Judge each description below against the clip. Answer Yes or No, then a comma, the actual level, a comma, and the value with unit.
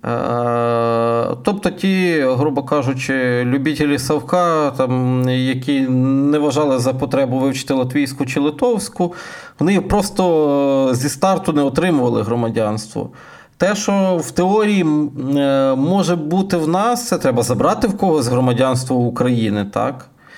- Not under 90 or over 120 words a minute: Yes, average, 110 wpm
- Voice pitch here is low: No, medium, 145 Hz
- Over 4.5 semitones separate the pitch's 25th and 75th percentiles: Yes, wide, 5.4 semitones